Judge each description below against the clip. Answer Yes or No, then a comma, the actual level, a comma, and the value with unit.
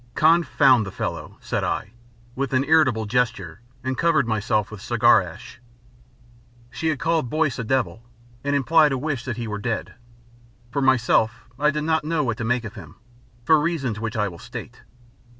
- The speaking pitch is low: Yes, low, 130 Hz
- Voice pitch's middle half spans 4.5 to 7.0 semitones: Yes, average, 5.2 semitones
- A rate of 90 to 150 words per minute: No, average, 180 wpm